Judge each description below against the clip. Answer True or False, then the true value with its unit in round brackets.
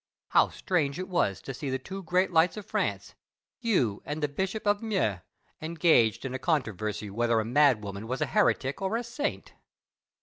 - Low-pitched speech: False (150 Hz)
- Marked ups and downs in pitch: True (8.3 semitones)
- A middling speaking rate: True (180 wpm)